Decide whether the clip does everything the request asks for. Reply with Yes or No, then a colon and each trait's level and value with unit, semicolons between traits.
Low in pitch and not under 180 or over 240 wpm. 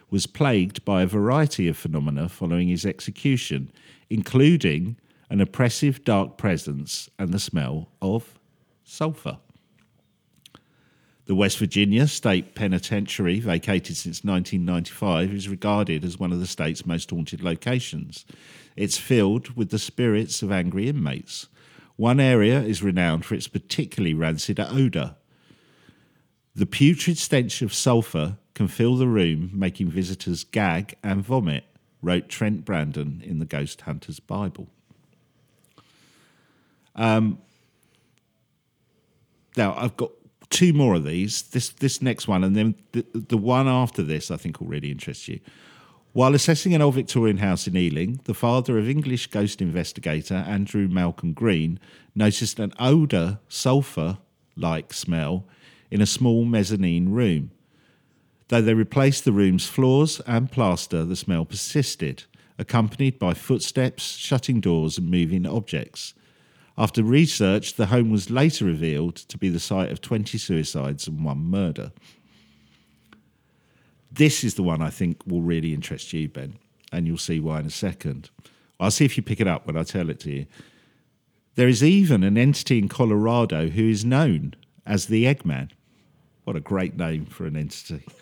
No: low, 105 Hz; average, 150 wpm